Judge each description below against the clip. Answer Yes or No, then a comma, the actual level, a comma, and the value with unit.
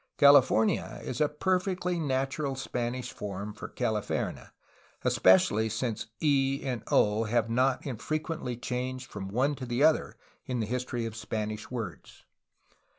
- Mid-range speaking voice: No, low, 125 Hz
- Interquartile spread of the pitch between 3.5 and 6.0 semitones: Yes, average, 3.9 semitones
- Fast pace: No, average, 145 wpm